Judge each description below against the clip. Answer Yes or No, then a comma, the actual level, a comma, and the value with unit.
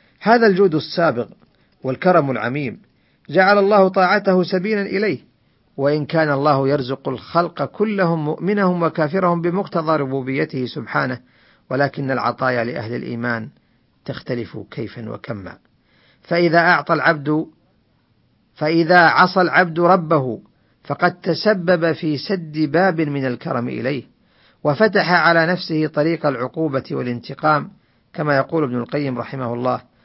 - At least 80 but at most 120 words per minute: Yes, average, 110 wpm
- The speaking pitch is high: No, medium, 155 Hz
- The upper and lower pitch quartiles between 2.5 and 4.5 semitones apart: No, average, 5.1 semitones